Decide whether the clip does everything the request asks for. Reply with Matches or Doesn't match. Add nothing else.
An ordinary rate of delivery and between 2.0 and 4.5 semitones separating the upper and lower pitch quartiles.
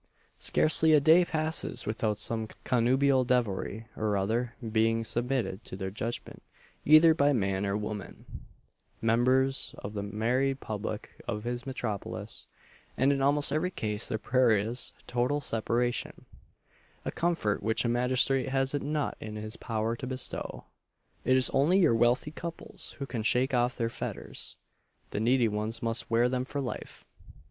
Matches